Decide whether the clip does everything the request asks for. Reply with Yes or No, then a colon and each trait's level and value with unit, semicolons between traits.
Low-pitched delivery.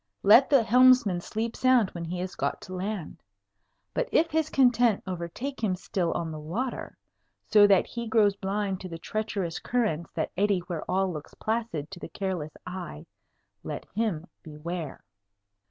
No: high, 195 Hz